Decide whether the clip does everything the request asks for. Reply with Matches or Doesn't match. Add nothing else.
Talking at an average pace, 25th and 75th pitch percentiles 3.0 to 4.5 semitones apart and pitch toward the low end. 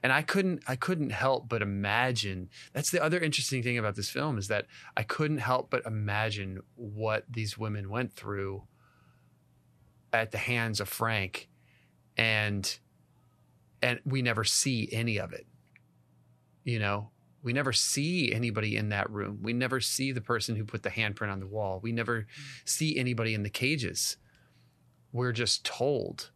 Matches